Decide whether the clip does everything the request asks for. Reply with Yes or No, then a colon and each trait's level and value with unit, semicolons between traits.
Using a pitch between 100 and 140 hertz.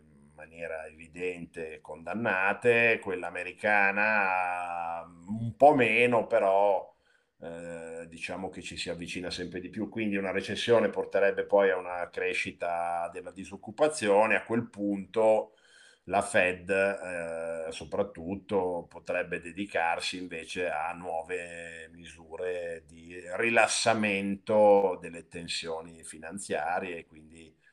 No: very low, 90 Hz